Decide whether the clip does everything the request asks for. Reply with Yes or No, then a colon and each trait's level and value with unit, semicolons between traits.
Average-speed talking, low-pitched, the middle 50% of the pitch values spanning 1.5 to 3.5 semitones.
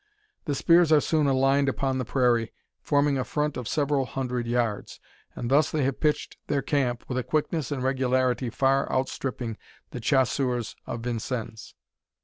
Yes: average, 160 wpm; low, 130 Hz; narrow, 2.5 semitones